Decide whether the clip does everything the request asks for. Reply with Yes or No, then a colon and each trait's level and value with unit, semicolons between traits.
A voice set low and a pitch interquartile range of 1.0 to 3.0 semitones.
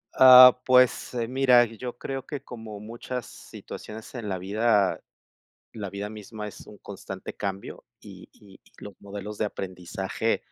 No: low, 105 Hz; average, 3.5 semitones